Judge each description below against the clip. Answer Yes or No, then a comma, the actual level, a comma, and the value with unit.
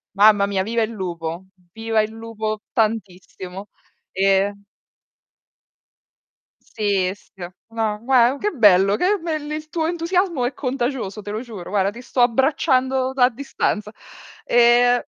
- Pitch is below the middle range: No, high, 225 Hz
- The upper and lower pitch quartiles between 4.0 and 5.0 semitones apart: Yes, average, 4.5 semitones